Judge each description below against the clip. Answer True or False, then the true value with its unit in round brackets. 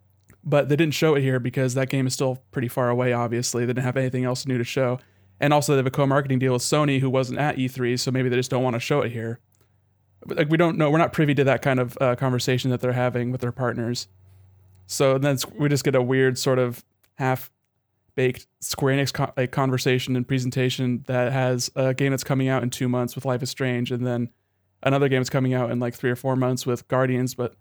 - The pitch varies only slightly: True (1.6 semitones)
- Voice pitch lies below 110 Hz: False (125 Hz)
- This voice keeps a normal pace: False (245 wpm)